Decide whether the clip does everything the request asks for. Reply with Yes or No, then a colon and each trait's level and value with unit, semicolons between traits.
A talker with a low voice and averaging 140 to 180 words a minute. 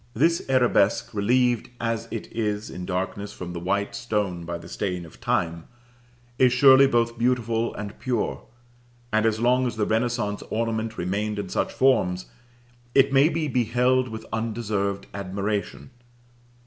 Yes: low, 110 Hz; average, 150 wpm